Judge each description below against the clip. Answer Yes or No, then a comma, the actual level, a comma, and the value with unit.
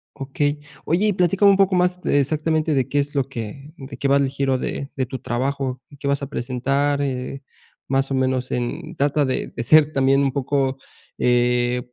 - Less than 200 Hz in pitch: Yes, medium, 140 Hz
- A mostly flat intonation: Yes, narrow, 2.1 semitones